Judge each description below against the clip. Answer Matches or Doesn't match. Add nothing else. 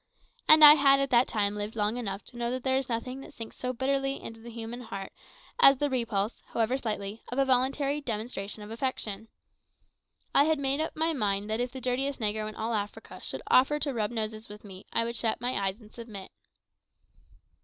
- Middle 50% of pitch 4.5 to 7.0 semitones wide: Doesn't match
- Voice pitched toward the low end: Doesn't match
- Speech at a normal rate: Doesn't match